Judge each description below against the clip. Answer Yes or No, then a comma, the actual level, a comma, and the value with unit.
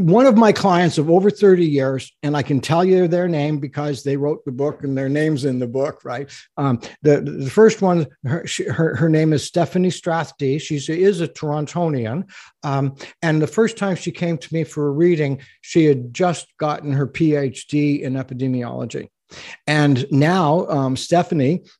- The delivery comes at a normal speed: Yes, average, 185 wpm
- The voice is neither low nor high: Yes, medium, 150 Hz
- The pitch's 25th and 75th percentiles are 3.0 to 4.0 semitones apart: Yes, average, 3.7 semitones